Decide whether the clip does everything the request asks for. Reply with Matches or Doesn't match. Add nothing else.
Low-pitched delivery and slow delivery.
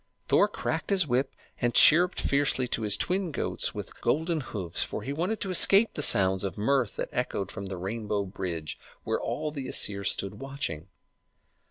Doesn't match